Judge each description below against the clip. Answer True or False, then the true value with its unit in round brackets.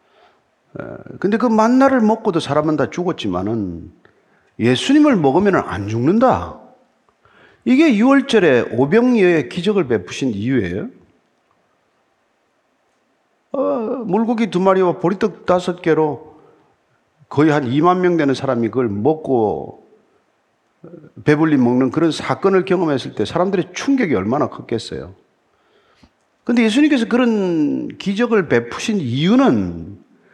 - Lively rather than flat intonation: True (8.0 semitones)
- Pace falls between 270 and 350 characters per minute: False (250 characters per minute)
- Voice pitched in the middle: True (180 Hz)